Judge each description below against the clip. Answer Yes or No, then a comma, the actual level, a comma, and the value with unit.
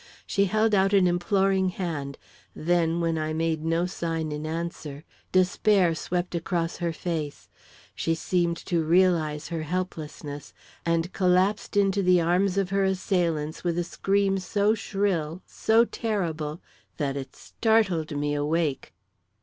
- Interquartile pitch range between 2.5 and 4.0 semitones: Yes, average, 3.2 semitones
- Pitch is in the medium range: Yes, medium, 175 Hz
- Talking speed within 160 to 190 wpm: No, average, 140 wpm